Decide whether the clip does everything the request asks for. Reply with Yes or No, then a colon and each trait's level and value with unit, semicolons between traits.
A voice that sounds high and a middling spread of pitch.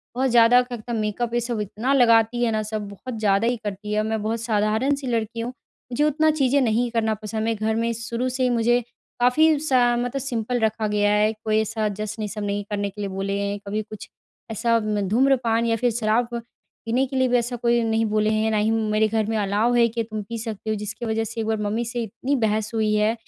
No: high, 225 Hz; narrow, 2.0 semitones